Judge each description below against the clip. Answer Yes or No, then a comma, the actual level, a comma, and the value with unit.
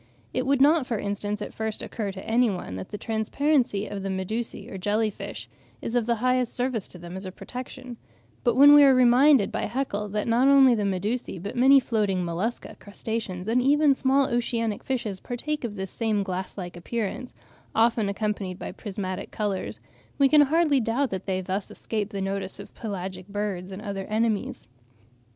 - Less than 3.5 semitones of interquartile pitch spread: No, average, 4.3 semitones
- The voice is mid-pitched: No, high, 215 Hz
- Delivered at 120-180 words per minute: No, average, 190 wpm